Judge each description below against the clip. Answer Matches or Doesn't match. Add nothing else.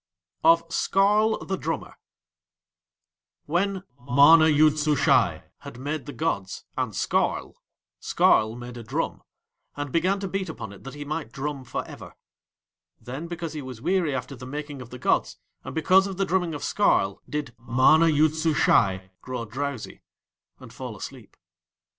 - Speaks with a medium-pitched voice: Matches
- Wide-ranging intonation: Doesn't match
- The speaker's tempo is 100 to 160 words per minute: Matches